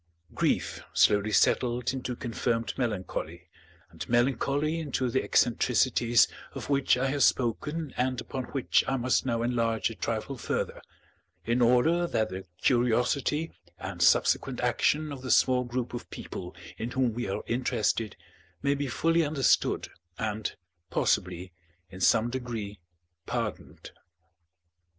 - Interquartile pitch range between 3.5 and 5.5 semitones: No, average, 2.7 semitones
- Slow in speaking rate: Yes, slow, 130 wpm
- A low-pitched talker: Yes, low, 125 Hz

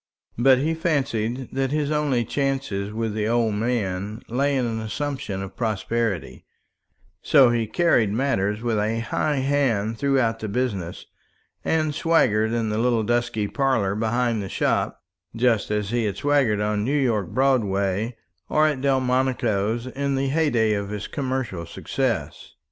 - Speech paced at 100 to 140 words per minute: No, average, 150 wpm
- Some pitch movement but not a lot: Yes, average, 4.1 semitones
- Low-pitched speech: Yes, low, 120 Hz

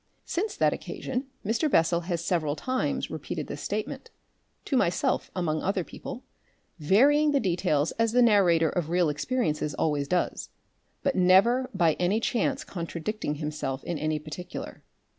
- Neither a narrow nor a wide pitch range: No, wide, 6.9 semitones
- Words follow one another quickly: No, average, 145 wpm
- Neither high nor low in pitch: Yes, medium, 180 Hz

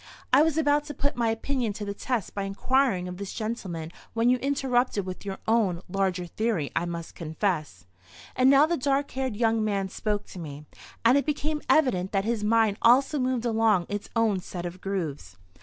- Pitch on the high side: Yes, high, 220 Hz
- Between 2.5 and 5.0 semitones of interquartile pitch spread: No, wide, 5.6 semitones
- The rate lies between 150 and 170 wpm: No, average, 190 wpm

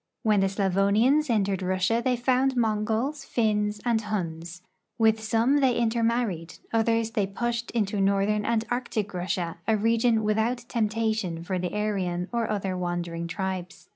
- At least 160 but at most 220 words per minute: No, average, 145 wpm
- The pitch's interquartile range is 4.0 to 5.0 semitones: No, average, 3.4 semitones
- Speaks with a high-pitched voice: Yes, high, 215 Hz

